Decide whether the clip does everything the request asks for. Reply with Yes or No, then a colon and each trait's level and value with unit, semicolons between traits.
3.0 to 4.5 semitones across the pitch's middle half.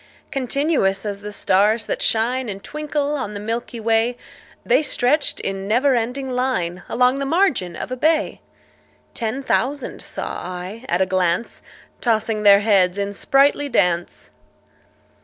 No: average, 5.1 semitones